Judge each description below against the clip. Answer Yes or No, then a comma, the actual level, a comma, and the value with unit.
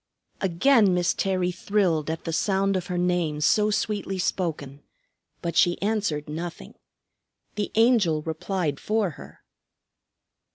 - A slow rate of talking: Yes, slow, 125 wpm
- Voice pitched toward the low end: No, medium, 180 Hz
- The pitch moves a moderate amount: Yes, average, 3.7 semitones